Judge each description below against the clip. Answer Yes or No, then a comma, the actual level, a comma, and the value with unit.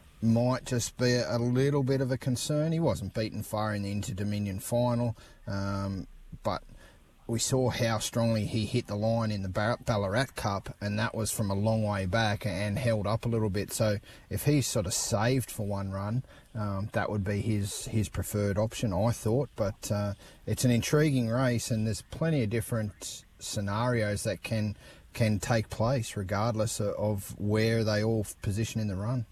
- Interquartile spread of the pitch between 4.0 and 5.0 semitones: No, average, 2.7 semitones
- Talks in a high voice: No, low, 110 Hz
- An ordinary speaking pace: Yes, average, 185 wpm